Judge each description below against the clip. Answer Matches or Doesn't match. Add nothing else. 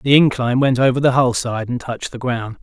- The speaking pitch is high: Doesn't match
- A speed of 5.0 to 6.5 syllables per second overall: Matches